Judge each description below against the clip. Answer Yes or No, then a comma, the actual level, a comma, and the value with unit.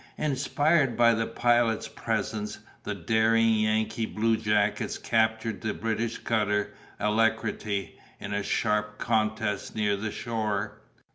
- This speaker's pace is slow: Yes, slow, 115 wpm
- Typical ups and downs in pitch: No, narrow, 1.3 semitones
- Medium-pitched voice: No, low, 110 Hz